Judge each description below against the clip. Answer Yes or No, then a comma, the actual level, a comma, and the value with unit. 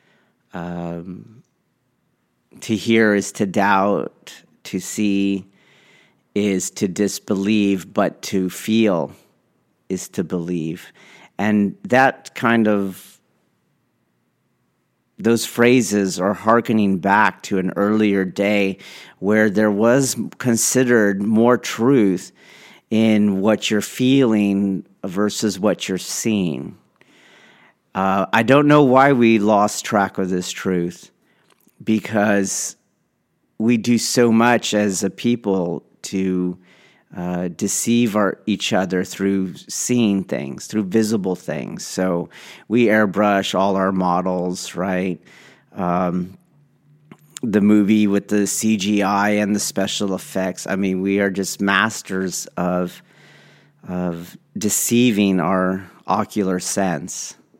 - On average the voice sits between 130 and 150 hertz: No, low, 100 Hz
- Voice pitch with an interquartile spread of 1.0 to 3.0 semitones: Yes, average, 2.7 semitones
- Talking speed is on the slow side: Yes, slow, 110 wpm